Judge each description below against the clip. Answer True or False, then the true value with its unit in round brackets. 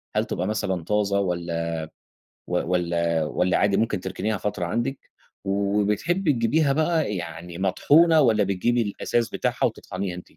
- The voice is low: True (100 Hz)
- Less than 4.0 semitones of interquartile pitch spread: False (4.8 semitones)